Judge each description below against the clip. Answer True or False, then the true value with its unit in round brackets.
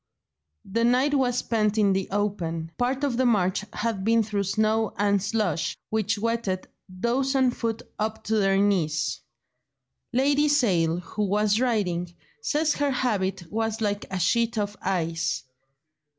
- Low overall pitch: False (215 Hz)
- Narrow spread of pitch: False (3.7 semitones)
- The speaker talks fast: False (150 wpm)